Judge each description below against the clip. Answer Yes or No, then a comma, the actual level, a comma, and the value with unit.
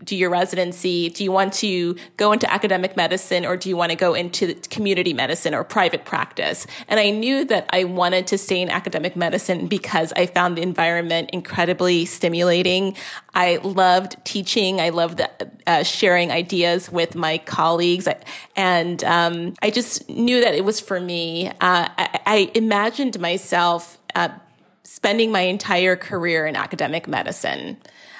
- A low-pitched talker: No, medium, 180 Hz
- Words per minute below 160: No, average, 165 wpm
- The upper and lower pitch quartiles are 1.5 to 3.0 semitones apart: Yes, narrow, 2.4 semitones